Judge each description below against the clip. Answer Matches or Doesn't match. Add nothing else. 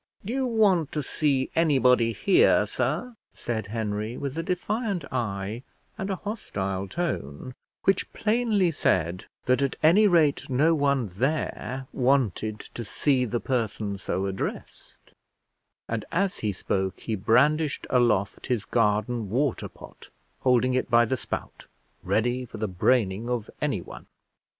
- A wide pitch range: Matches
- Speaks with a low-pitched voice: Matches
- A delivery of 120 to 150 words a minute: Matches